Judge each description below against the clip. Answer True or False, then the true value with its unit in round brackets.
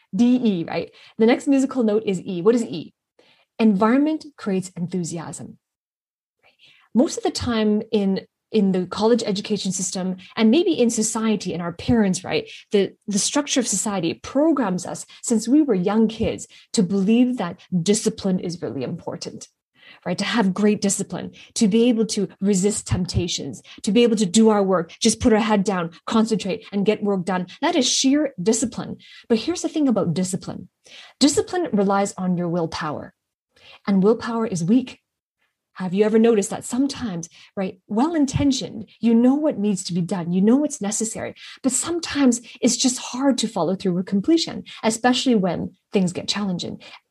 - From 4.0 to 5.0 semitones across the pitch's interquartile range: True (4.3 semitones)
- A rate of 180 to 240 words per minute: False (170 wpm)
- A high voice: True (215 Hz)